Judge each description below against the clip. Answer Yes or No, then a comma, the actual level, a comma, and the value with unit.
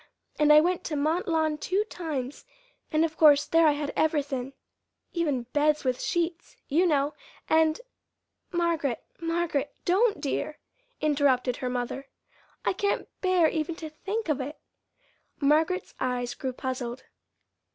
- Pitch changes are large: No, average, 3.4 semitones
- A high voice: Yes, very high, 305 Hz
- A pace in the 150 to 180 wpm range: No, average, 140 wpm